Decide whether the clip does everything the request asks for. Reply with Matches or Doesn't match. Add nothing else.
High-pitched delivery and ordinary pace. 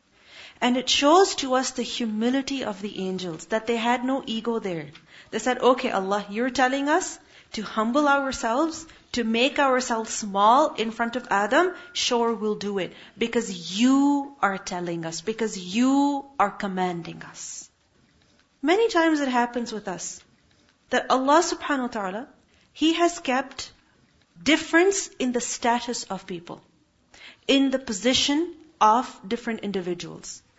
Matches